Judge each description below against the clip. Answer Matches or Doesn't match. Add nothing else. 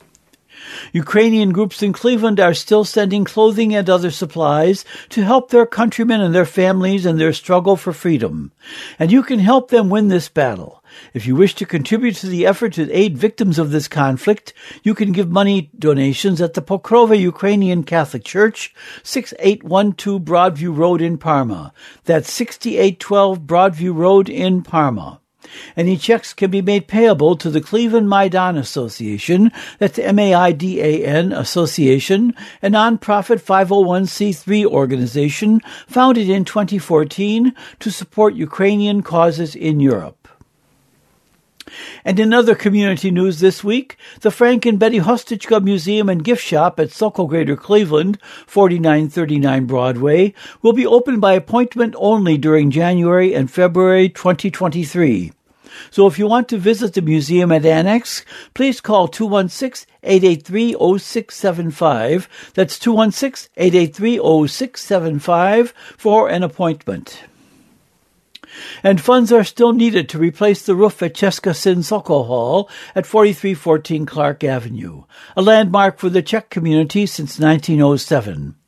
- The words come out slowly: Matches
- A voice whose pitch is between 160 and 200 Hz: Matches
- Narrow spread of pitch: Doesn't match